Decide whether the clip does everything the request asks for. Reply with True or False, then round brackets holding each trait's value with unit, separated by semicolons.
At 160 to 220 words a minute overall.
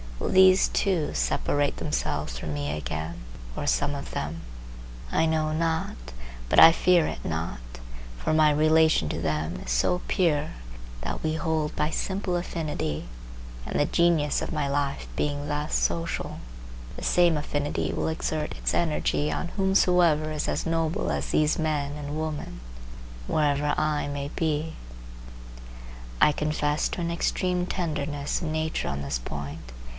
False (150 wpm)